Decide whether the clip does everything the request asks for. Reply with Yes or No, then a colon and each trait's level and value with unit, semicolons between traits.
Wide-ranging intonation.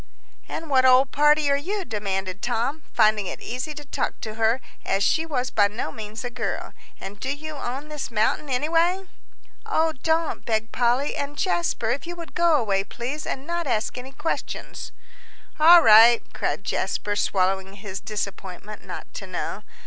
Yes: wide, 6.2 semitones